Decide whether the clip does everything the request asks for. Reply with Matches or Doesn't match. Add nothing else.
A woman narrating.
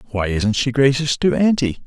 Doesn't match